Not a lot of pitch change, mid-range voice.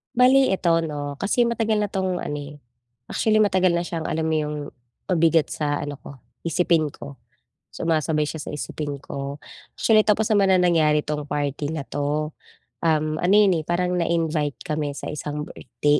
No: average, 3.6 semitones; medium, 160 Hz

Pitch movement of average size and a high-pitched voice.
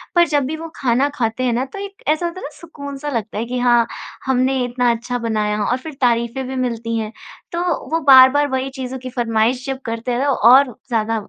Yes: average, 3.0 semitones; very high, 255 Hz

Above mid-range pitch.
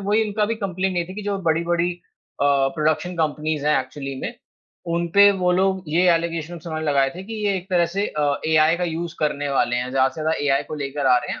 No: medium, 165 Hz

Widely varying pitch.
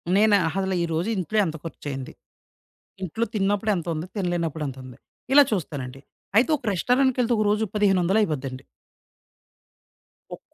Yes: wide, 5.7 semitones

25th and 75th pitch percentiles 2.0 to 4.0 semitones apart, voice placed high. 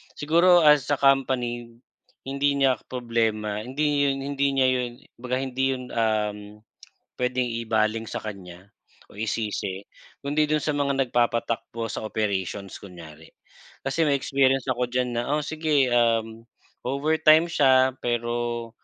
No: average, 3.7 semitones; low, 125 Hz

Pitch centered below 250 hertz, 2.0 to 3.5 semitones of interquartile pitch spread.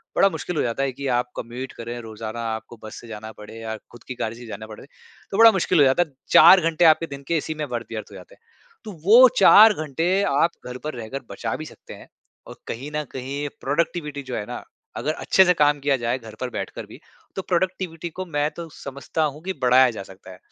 No: medium, 140 Hz; wide, 6.0 semitones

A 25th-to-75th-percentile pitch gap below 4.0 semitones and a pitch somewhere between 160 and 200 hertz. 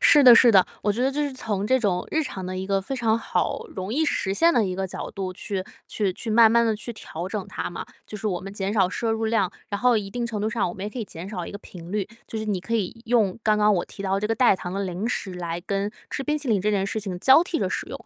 No: average, 3.3 semitones; high, 210 Hz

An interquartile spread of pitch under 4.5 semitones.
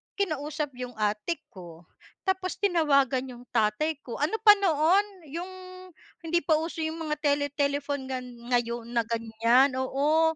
No: average, 4.9 semitones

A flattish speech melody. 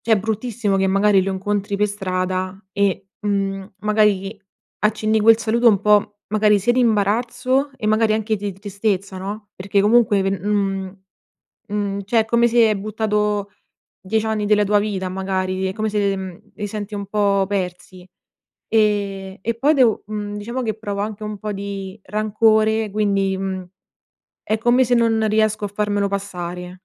Yes: narrow, 1.8 semitones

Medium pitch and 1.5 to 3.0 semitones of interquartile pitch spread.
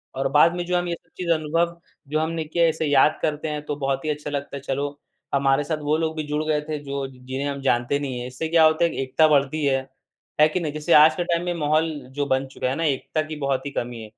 Yes: medium, 150 Hz; narrow, 2.6 semitones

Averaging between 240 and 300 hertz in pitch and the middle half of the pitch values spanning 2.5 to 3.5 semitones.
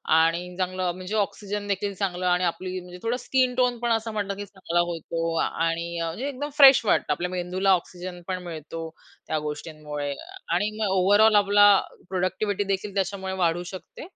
No: medium, 185 Hz; average, 2.8 semitones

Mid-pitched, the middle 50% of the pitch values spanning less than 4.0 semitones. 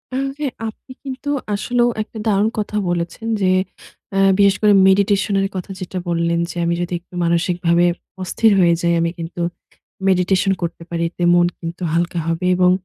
Yes: medium, 180 Hz; average, 2.9 semitones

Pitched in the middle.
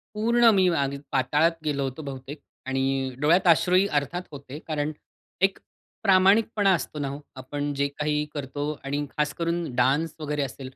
Yes: medium, 150 Hz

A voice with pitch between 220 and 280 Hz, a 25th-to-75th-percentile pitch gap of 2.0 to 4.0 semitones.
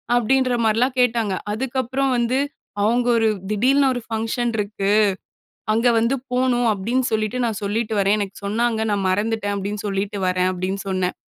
Yes: high, 225 Hz; average, 3.3 semitones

